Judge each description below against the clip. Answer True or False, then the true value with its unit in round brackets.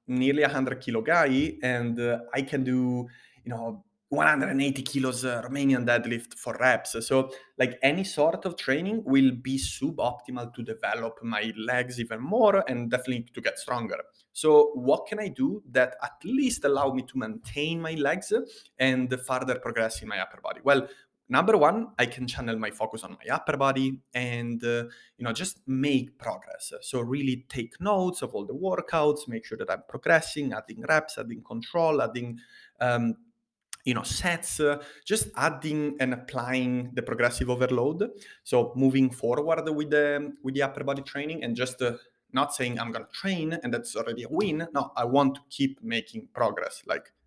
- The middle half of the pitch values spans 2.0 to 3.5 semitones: False (4.2 semitones)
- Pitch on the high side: False (130 Hz)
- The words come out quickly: False (180 wpm)